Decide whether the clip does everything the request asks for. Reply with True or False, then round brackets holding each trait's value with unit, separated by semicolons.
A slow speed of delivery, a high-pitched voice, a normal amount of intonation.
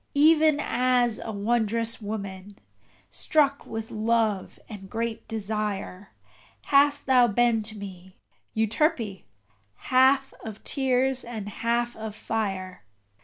True (110 wpm; 225 Hz; 3.6 semitones)